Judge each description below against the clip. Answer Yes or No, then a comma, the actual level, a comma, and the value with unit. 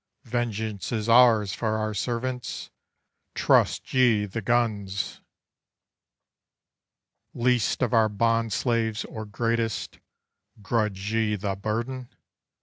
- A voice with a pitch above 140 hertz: No, low, 110 Hz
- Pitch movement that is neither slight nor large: No, narrow, 2.1 semitones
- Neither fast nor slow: No, slow, 100 wpm